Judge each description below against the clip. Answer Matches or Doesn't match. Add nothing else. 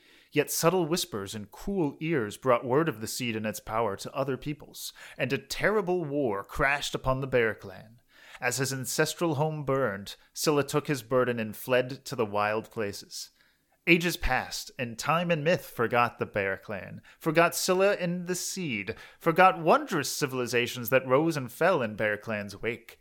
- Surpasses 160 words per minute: Matches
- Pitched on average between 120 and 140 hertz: Matches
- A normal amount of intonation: Doesn't match